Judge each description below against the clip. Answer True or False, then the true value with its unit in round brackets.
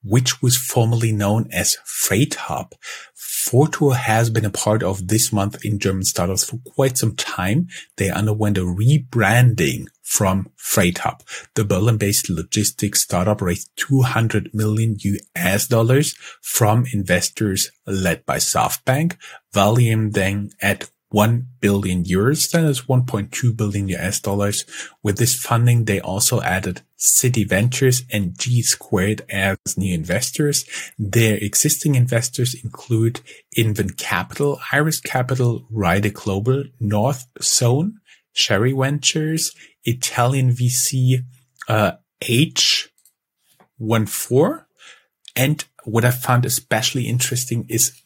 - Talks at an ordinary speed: False (120 wpm)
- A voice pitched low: True (115 Hz)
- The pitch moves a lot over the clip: False (3.8 semitones)